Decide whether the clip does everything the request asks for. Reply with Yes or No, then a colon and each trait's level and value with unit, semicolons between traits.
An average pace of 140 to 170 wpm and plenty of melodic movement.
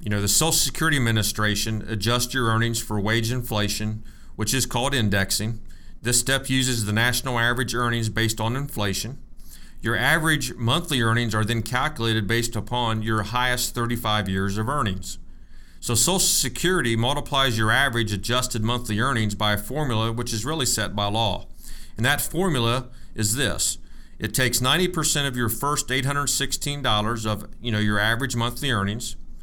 No: average, 160 wpm; average, 3.1 semitones